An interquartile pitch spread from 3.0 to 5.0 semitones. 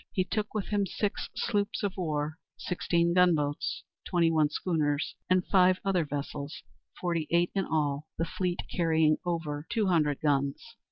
Yes: average, 3.6 semitones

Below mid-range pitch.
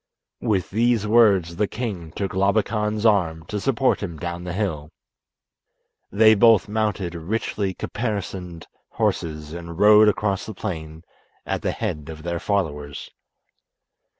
Yes: very low, 95 Hz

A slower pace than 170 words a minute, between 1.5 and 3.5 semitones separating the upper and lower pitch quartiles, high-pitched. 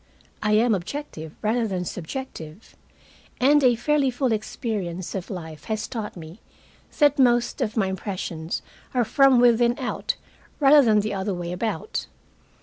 No: average, 145 wpm; wide, 5.4 semitones; high, 220 Hz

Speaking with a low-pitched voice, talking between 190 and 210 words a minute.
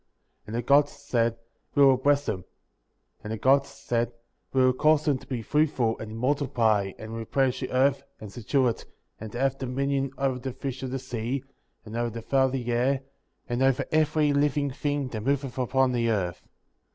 Yes: low, 130 Hz; average, 200 wpm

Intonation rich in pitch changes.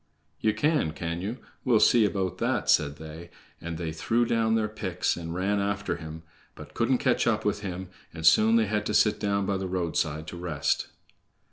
No: average, 4.3 semitones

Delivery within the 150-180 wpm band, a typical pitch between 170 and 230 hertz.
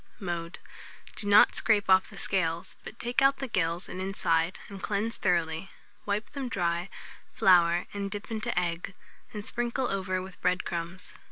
Yes: average, 170 wpm; high, 190 Hz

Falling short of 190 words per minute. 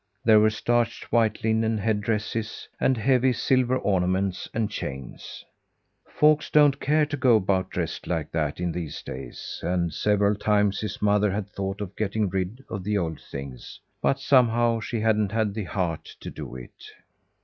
Yes: average, 170 wpm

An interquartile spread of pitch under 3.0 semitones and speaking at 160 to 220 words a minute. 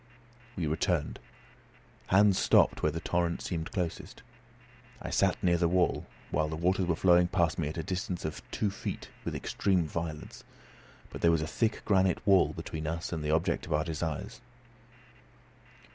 Yes: narrow, 2.6 semitones; average, 170 wpm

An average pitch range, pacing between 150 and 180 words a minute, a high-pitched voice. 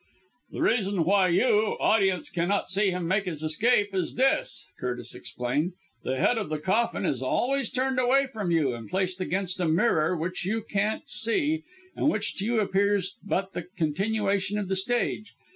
Yes: average, 4.1 semitones; average, 175 wpm; high, 195 Hz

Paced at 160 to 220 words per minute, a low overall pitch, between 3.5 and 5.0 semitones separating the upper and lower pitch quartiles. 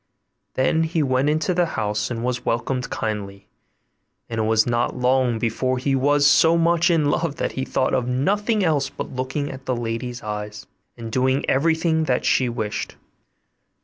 Yes: average, 175 wpm; low, 130 Hz; average, 4.2 semitones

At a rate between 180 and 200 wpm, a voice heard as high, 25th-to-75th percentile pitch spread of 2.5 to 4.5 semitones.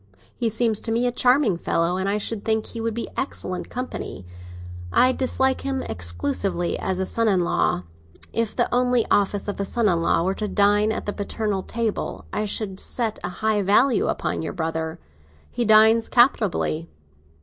Yes: average, 185 wpm; high, 210 Hz; average, 3.7 semitones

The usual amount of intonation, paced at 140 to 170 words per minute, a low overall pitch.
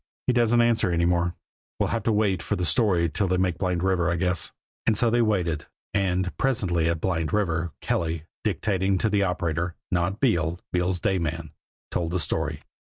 No: average, 3.1 semitones; average, 190 wpm; very low, 90 Hz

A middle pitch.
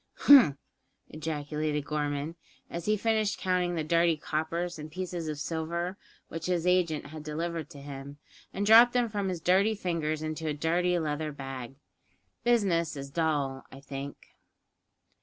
Yes: medium, 160 Hz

